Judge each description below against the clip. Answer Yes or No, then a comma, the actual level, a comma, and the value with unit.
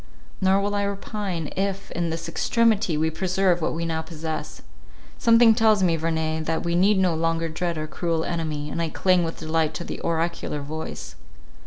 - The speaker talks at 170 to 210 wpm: Yes, average, 185 wpm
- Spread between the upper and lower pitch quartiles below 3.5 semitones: Yes, average, 3.0 semitones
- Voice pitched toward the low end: No, medium, 165 Hz